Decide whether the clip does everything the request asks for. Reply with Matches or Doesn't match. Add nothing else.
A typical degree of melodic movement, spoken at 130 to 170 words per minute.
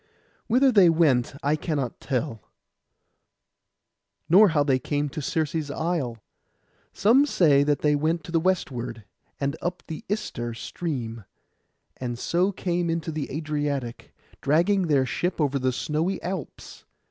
Matches